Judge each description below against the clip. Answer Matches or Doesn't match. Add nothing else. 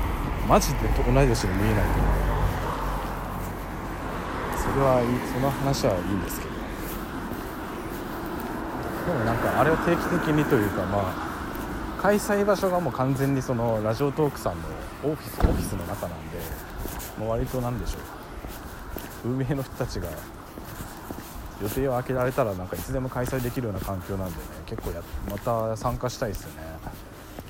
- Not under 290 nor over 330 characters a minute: Matches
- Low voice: Matches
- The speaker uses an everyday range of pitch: Doesn't match